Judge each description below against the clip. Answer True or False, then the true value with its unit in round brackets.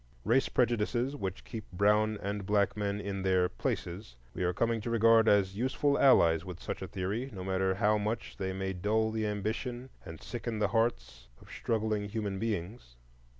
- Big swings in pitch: False (3.1 semitones)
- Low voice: True (105 Hz)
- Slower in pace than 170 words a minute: False (180 wpm)